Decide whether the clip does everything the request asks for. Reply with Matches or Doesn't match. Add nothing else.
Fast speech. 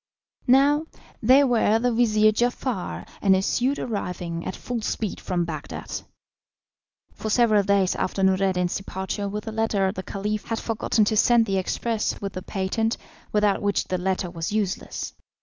Doesn't match